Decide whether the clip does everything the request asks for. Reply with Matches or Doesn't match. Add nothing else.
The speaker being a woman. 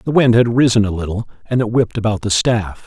Doesn't match